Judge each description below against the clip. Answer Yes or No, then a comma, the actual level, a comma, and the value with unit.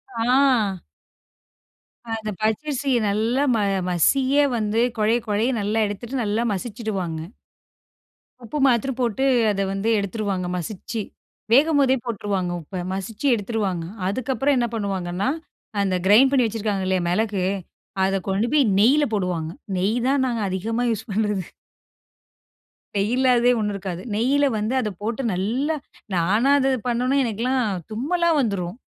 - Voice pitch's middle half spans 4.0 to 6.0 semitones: Yes, average, 4.3 semitones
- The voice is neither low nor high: No, high, 220 Hz